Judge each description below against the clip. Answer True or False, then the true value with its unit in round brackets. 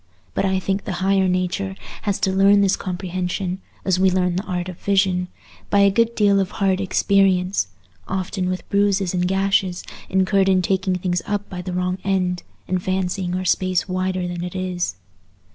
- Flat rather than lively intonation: True (1.3 semitones)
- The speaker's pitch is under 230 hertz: True (185 Hz)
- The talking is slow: False (180 wpm)